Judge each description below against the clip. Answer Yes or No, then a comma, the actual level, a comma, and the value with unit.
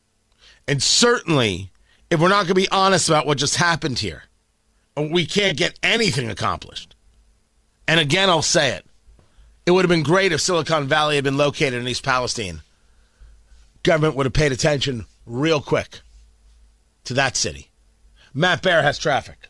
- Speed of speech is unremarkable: Yes, average, 160 wpm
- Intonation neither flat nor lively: No, wide, 8.1 semitones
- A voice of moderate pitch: Yes, medium, 145 Hz